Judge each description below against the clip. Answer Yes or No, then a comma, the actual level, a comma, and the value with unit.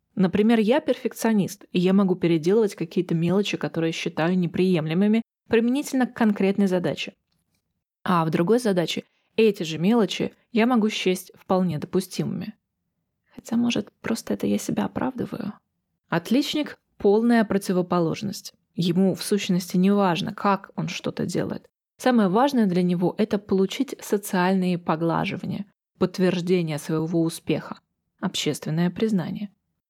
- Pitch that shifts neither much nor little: Yes, average, 3.7 semitones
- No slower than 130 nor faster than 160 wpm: No, average, 120 wpm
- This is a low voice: No, high, 195 Hz